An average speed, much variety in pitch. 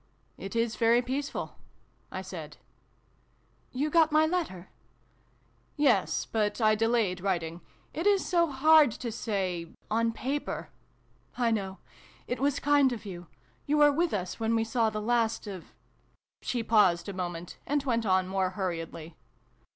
Yes: average, 165 wpm; wide, 6.3 semitones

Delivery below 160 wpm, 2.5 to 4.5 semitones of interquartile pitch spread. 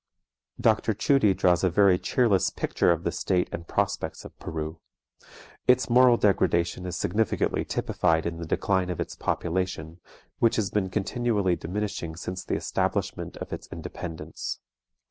Yes: average, 145 wpm; average, 3.8 semitones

